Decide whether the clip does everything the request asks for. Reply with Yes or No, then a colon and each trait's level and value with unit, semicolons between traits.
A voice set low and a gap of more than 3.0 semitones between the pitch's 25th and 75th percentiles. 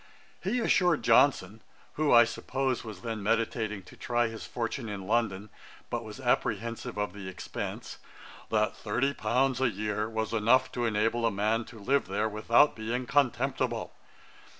No: low, 115 Hz; average, 2.7 semitones